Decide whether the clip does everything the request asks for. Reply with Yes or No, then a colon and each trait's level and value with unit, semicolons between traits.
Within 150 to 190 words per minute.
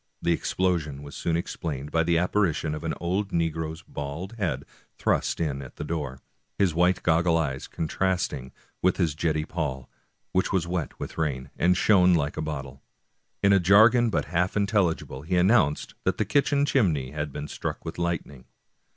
Yes: average, 175 wpm